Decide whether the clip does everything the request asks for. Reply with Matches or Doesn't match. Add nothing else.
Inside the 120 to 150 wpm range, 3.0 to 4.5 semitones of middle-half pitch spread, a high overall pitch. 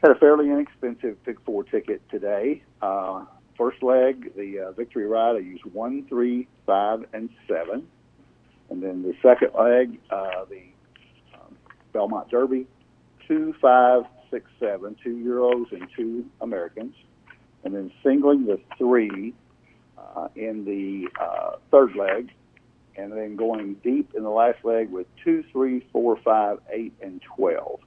Doesn't match